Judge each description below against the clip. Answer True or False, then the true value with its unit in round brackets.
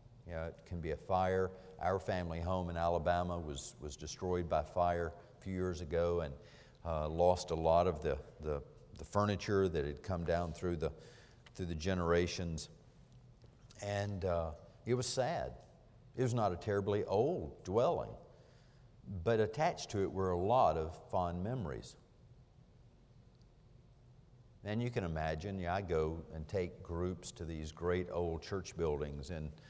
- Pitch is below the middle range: True (90 Hz)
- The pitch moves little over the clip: False (4.4 semitones)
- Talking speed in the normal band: True (160 wpm)